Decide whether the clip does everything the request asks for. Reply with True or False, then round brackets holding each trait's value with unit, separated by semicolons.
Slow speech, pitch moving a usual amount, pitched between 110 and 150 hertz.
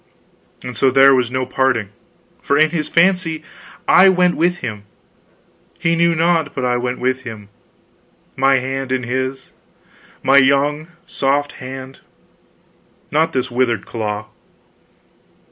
True (130 wpm; 3.6 semitones; 135 Hz)